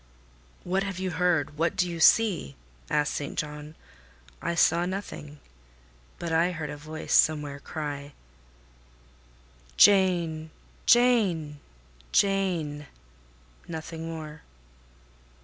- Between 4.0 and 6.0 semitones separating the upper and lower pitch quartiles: No, average, 3.3 semitones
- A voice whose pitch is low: No, medium, 160 Hz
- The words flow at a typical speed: No, slow, 95 wpm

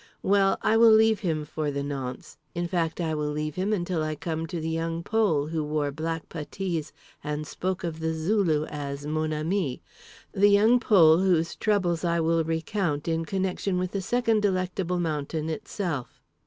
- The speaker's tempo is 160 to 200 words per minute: Yes, average, 175 wpm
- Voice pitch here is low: No, medium, 165 Hz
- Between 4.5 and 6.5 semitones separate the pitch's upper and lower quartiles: No, average, 3.6 semitones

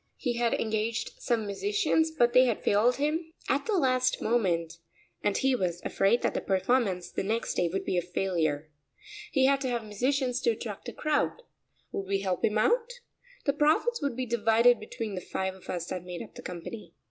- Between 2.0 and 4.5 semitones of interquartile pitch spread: No, wide, 5.5 semitones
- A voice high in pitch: Yes, high, 230 Hz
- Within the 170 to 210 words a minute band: Yes, average, 200 wpm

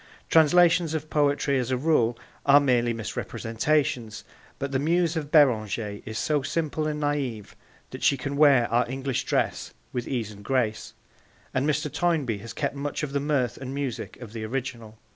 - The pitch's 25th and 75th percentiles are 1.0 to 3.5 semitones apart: No, average, 4.0 semitones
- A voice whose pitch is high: No, low, 135 Hz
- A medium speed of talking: Yes, average, 175 wpm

